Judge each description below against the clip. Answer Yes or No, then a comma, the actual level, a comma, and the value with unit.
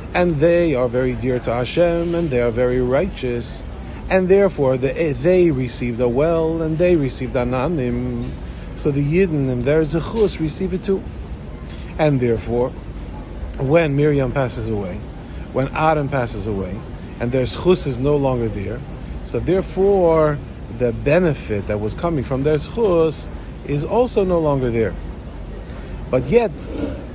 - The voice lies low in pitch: Yes, low, 130 Hz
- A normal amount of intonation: No, wide, 6.5 semitones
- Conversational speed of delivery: Yes, average, 145 wpm